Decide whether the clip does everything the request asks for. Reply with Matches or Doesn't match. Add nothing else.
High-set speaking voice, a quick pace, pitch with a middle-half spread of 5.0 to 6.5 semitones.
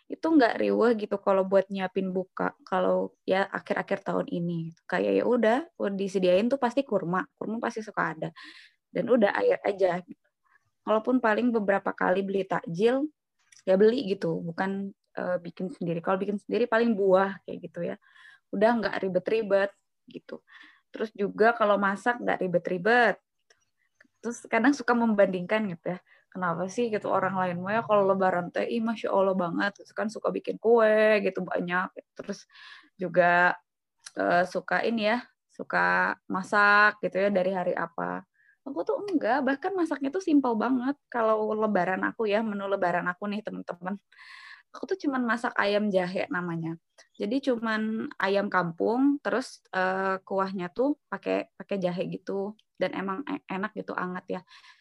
Doesn't match